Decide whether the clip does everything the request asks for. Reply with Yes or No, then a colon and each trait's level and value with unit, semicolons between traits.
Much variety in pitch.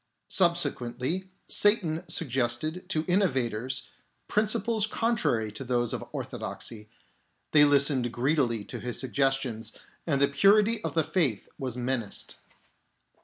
Yes: wide, 6.5 semitones